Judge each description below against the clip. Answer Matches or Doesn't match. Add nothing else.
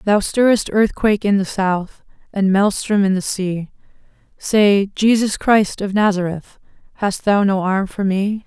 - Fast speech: Doesn't match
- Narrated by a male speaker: Doesn't match